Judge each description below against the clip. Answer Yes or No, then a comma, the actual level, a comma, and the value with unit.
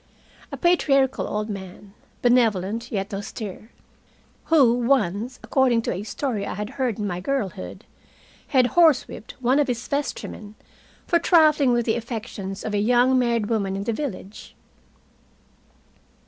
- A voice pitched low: No, high, 230 Hz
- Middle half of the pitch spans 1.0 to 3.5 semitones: No, average, 4.2 semitones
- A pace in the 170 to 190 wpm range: No, average, 140 wpm